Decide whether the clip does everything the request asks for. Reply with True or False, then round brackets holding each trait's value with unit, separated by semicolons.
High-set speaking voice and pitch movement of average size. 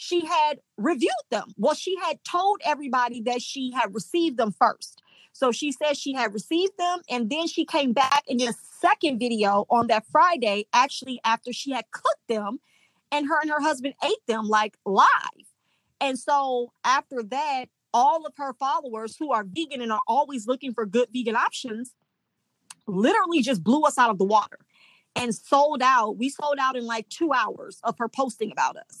True (260 Hz; 4.5 semitones)